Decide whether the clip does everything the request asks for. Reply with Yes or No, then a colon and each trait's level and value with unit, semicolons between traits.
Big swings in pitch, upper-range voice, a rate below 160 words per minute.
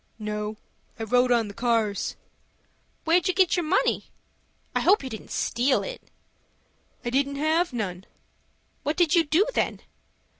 Yes: wide, 6.9 semitones; very high, 260 Hz; average, 150 wpm